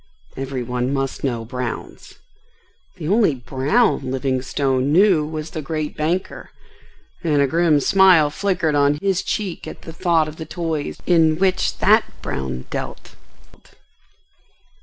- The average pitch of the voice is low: No, medium, 155 Hz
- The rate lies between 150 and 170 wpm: No, slow, 135 wpm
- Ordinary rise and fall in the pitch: Yes, average, 4.4 semitones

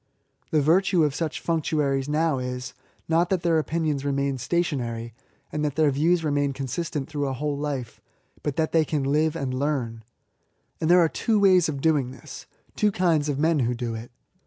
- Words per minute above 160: Yes, average, 190 wpm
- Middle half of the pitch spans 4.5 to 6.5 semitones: No, average, 3.2 semitones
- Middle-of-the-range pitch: Yes, medium, 150 Hz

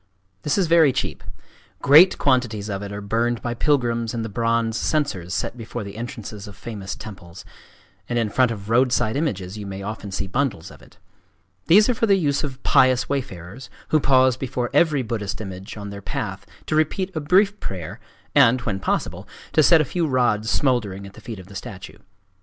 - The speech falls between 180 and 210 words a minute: Yes, average, 195 wpm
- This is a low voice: Yes, low, 115 Hz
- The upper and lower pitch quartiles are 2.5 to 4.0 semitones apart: No, wide, 5.4 semitones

